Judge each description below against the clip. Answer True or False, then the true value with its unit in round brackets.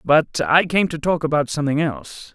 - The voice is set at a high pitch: False (150 Hz)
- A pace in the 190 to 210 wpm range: True (205 wpm)